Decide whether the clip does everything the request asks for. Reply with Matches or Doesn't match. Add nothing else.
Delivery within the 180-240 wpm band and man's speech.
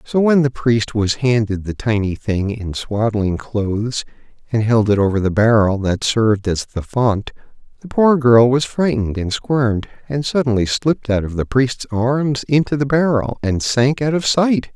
Matches